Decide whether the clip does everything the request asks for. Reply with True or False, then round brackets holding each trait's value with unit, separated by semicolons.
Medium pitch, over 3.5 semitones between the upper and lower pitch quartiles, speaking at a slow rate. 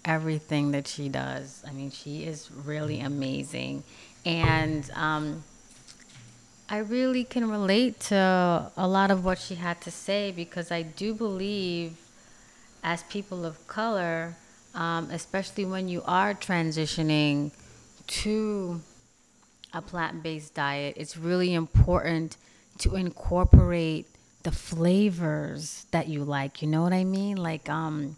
True (165 Hz; 3.9 semitones; 130 wpm)